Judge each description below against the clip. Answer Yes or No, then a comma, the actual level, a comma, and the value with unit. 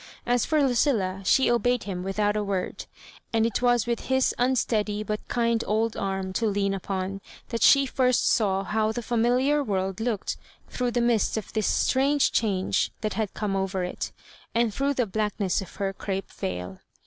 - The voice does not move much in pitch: No, average, 3.7 semitones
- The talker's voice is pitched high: Yes, high, 215 Hz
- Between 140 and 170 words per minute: No, average, 180 wpm